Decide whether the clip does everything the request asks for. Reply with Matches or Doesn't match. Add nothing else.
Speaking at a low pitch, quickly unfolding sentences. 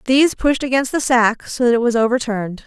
Doesn't match